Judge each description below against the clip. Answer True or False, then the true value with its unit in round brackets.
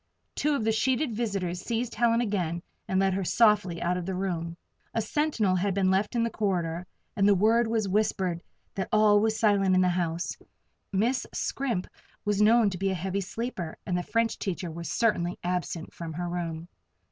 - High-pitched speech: True (195 Hz)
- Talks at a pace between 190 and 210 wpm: True (195 wpm)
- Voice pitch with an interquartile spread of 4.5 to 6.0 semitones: False (3.8 semitones)